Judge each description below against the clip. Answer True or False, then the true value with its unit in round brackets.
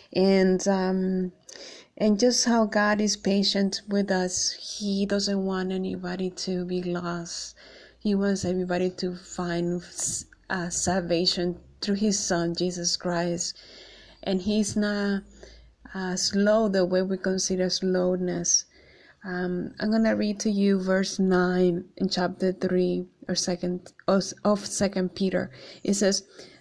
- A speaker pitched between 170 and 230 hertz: True (185 Hz)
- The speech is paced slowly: True (130 wpm)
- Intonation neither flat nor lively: False (1.8 semitones)